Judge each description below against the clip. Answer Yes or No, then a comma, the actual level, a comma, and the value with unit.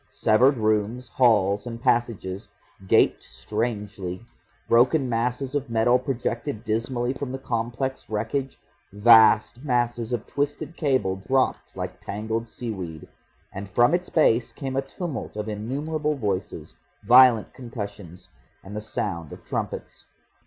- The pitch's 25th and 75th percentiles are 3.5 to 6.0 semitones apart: Yes, average, 3.8 semitones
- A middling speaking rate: No, slow, 125 wpm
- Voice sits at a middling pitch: No, low, 115 Hz